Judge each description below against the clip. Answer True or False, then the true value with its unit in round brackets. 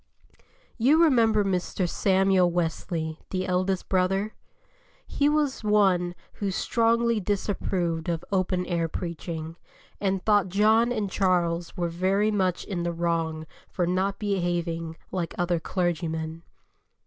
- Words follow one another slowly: True (125 wpm)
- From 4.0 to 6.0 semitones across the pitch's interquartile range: False (3.1 semitones)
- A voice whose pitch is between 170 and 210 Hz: True (185 Hz)